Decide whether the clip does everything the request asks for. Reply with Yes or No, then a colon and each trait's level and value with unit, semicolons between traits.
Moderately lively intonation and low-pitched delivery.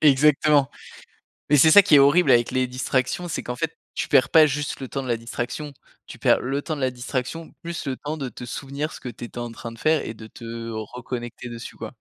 Yes: average, 3.7 semitones; low, 130 Hz